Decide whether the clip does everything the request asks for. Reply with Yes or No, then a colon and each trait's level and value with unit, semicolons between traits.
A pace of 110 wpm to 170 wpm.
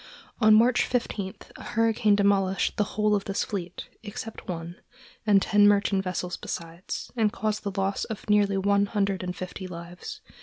Yes: average, 165 wpm